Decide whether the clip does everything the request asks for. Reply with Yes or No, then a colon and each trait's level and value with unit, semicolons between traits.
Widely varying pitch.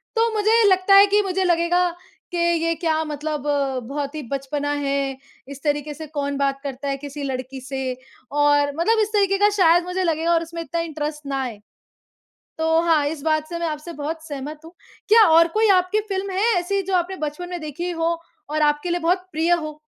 No: average, 3.5 semitones